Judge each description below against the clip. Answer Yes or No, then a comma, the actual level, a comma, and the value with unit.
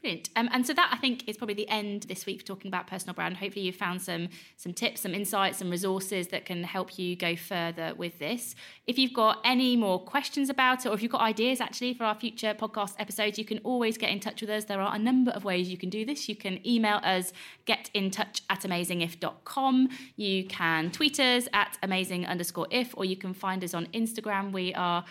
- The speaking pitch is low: No, high, 205 Hz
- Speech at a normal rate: No, fast, 230 wpm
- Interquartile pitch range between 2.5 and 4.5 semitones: Yes, average, 4.0 semitones